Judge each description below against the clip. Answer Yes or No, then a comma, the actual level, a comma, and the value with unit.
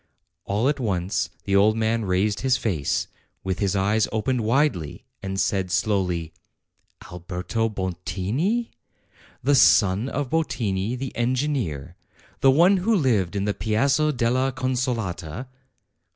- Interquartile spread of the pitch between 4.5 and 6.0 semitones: Yes, wide, 5.5 semitones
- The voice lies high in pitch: No, low, 110 Hz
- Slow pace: Yes, slow, 125 wpm